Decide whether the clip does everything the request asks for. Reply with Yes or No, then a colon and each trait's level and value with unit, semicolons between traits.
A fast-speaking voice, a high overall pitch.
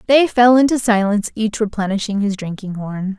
No: average, 170 wpm; high, 215 Hz